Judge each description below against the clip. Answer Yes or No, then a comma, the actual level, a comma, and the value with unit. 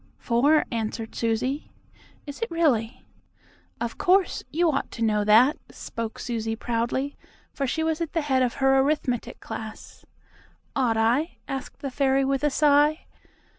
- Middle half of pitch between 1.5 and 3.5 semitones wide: No, average, 4.3 semitones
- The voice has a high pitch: Yes, very high, 265 Hz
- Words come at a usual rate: Yes, average, 150 wpm